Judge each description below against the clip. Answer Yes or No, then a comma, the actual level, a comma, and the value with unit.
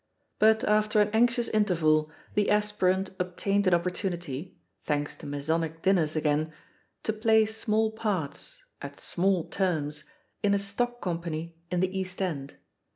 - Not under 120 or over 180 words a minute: Yes, average, 150 wpm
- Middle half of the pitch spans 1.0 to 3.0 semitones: No, average, 4.7 semitones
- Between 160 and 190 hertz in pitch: Yes, medium, 185 Hz